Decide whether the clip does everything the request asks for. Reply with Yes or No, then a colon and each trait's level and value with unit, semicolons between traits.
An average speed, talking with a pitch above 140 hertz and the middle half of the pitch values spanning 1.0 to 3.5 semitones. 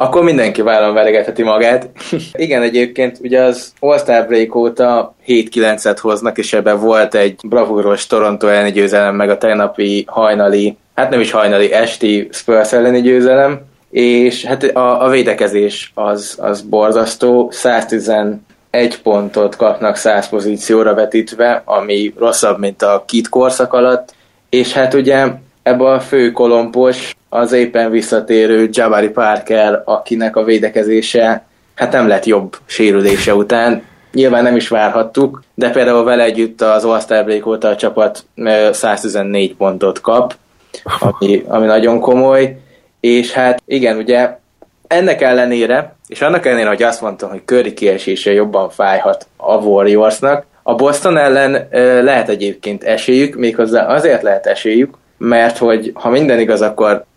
No: average, 140 wpm; low, 115 Hz; average, 2.8 semitones